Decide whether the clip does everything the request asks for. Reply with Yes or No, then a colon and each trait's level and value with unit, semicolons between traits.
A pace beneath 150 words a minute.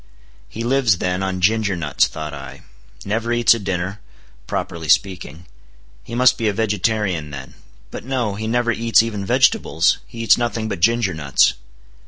No: average, 165 wpm